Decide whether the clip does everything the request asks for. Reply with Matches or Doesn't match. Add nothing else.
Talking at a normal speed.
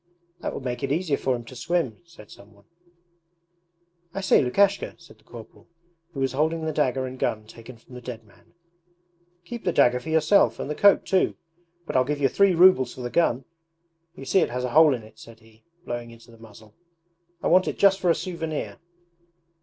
Doesn't match